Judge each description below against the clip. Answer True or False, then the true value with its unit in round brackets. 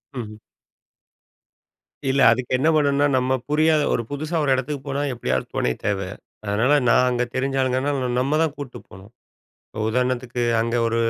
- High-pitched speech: False (130 Hz)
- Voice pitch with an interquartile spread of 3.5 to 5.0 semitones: False (3.0 semitones)